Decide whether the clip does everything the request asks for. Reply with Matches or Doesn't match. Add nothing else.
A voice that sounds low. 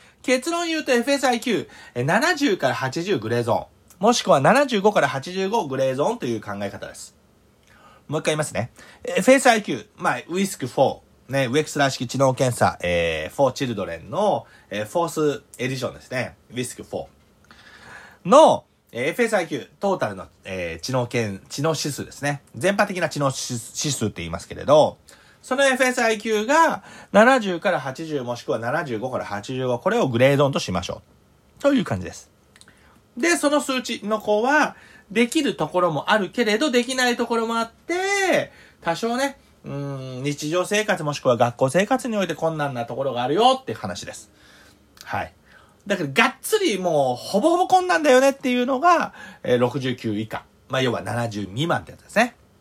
Doesn't match